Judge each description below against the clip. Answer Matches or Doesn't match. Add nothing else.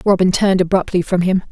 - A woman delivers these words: Matches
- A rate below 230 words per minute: Matches